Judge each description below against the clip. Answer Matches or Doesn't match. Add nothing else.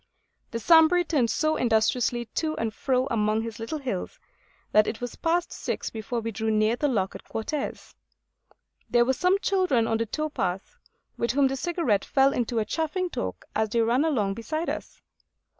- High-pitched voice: Matches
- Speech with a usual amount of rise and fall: Doesn't match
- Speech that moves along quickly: Doesn't match